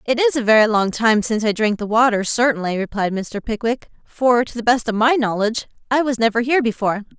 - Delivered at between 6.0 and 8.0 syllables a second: Yes, 6.1 syllables/s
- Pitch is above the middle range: Yes, high, 230 Hz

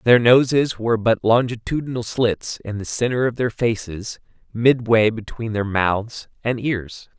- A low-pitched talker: Yes, low, 115 Hz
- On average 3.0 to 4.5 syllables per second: Yes, 4.2 syllables/s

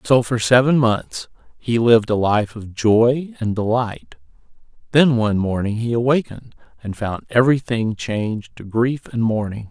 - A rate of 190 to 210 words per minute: No, average, 155 wpm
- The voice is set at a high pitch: No, low, 115 Hz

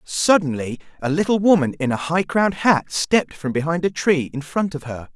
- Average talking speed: No, fast, 210 wpm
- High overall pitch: No, medium, 160 Hz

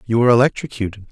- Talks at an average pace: Yes, average, 160 wpm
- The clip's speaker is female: No, male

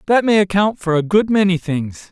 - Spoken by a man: Yes, male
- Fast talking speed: Yes, fast, 225 wpm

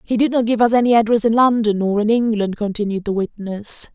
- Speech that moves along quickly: Yes, fast, 230 wpm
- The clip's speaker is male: No, female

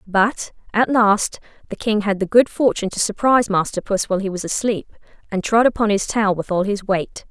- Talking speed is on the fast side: Yes, fast, 215 wpm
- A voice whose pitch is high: Yes, high, 210 Hz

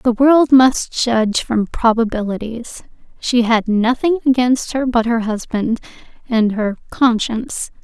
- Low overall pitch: No, high, 235 Hz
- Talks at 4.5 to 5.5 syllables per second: No, 4.0 syllables/s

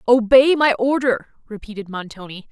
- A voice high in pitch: Yes, high, 230 Hz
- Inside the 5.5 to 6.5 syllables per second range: No, 4.9 syllables/s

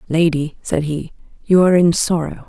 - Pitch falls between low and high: Yes, medium, 165 Hz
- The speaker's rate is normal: Yes, average, 170 wpm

